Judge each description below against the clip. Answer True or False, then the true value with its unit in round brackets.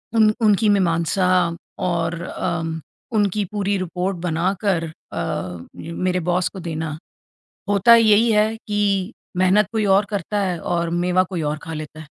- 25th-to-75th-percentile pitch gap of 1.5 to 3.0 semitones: False (3.7 semitones)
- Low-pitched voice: False (185 Hz)